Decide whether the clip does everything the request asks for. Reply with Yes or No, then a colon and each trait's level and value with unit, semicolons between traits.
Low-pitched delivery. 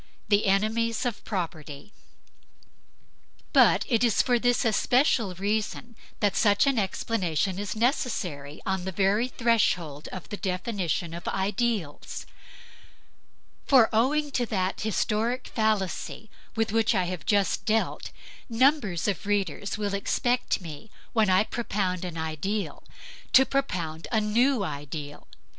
No: high, 205 Hz